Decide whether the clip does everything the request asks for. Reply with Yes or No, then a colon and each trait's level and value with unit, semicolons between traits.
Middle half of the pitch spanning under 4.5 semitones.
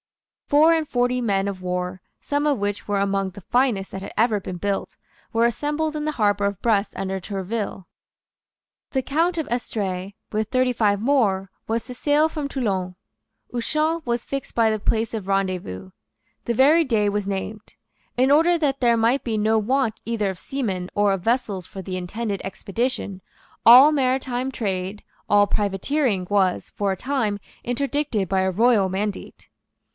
No: average, 5.0 semitones